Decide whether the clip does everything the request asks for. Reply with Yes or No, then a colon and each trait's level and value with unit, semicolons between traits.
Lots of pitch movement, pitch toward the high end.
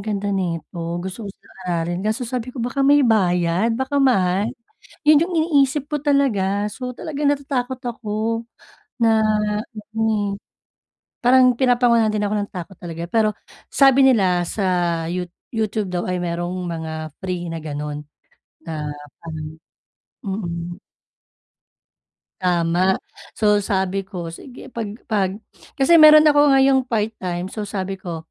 Yes: wide, 5.9 semitones; high, 205 Hz